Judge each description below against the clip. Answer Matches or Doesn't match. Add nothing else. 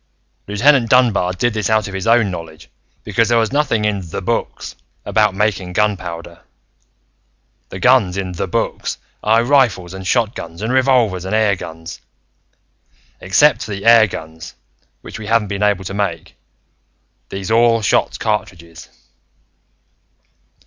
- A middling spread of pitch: Matches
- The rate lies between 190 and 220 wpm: Doesn't match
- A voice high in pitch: Doesn't match